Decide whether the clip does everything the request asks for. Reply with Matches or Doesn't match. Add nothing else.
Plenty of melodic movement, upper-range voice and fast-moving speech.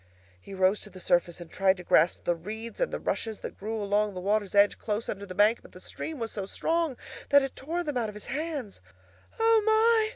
Matches